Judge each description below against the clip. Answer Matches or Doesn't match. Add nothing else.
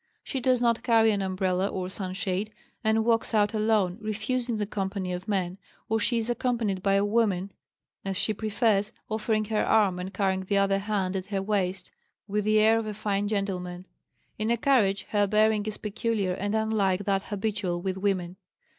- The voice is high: Matches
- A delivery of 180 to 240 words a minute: Matches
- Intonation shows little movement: Matches